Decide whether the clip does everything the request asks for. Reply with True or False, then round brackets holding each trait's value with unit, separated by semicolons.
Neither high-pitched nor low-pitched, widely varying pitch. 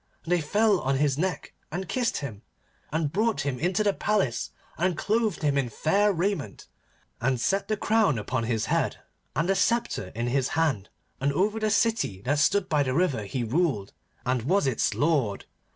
True (155 Hz; 7.5 semitones)